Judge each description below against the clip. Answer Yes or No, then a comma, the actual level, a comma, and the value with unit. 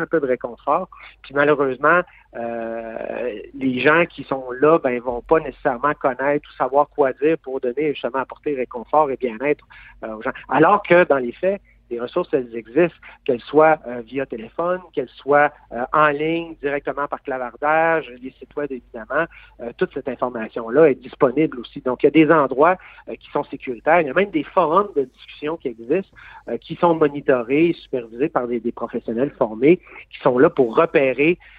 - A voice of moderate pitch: Yes, medium, 145 Hz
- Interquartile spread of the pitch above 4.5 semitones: No, average, 3.9 semitones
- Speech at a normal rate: Yes, average, 190 wpm